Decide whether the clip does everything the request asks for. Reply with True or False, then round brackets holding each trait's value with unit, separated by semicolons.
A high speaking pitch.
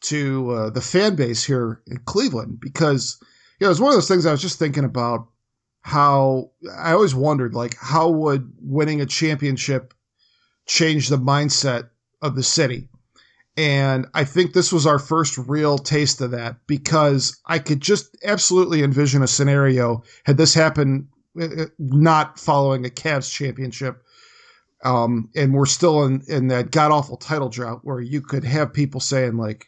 False (140 Hz)